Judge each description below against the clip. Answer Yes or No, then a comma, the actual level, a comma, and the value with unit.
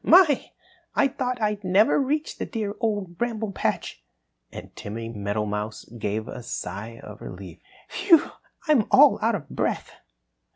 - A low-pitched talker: No, high, 200 Hz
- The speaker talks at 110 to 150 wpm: Yes, average, 140 wpm